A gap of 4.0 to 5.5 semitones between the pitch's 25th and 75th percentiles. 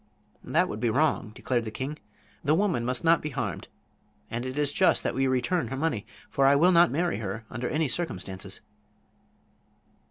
Yes: average, 5.0 semitones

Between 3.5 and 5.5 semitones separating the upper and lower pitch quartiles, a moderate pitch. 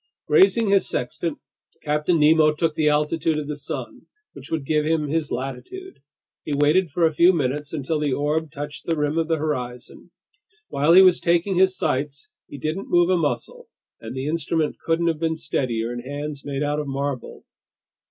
No: narrow, 2.4 semitones; medium, 150 Hz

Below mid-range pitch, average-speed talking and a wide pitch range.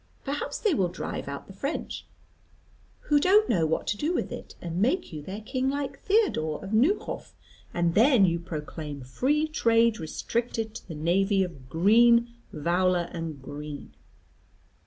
No: high, 195 Hz; average, 155 wpm; wide, 7.8 semitones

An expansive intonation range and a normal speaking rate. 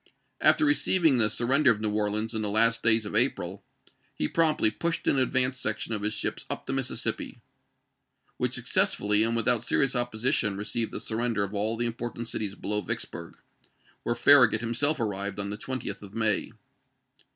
No: average, 2.9 semitones; average, 175 wpm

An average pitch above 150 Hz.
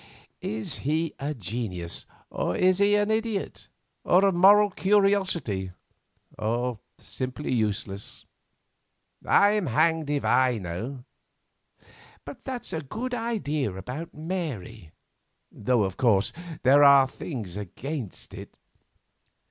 No: medium, 140 Hz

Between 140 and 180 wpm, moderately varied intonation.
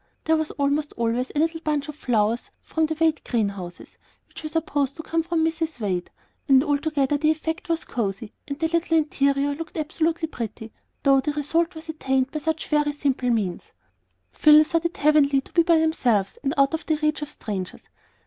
No: average, 195 wpm; average, 3.3 semitones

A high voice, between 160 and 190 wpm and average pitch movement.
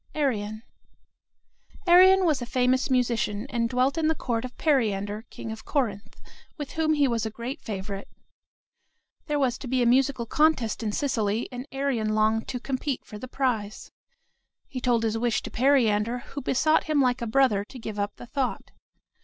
Yes: high, 245 Hz; average, 180 wpm; average, 3.8 semitones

